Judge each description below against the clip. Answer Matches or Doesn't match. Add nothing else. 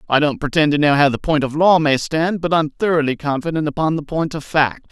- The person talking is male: Matches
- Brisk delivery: Matches